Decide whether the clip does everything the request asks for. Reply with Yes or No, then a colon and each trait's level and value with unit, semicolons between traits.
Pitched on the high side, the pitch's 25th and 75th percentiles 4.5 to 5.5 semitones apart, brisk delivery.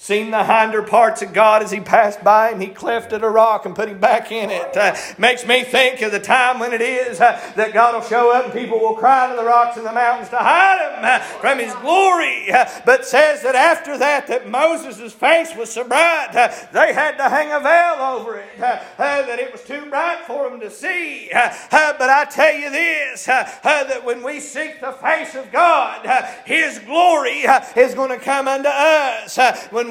Yes: very high, 260 Hz; average, 4.9 semitones; fast, 230 wpm